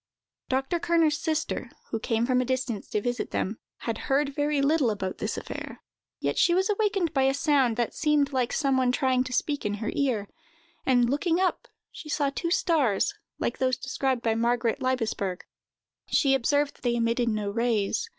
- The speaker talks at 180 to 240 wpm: Yes, average, 185 wpm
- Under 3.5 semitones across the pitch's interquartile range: No, average, 3.9 semitones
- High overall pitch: Yes, very high, 260 Hz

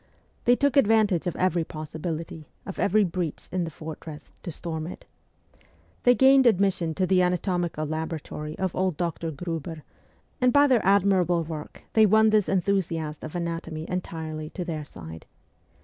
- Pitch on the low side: No, medium, 175 Hz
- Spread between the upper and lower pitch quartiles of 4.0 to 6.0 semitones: No, average, 3.6 semitones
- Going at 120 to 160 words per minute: Yes, average, 155 wpm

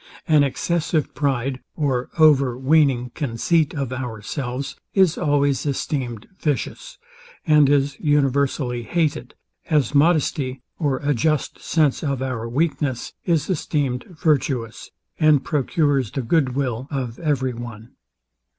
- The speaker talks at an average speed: No, slow, 115 wpm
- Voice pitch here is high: No, medium, 140 Hz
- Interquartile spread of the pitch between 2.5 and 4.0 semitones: Yes, average, 3.2 semitones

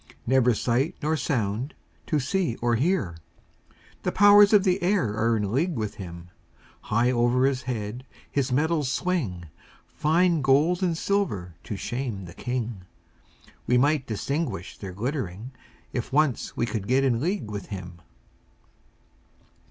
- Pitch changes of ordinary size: No, wide, 6.5 semitones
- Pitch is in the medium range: No, low, 125 Hz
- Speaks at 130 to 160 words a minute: Yes, average, 145 wpm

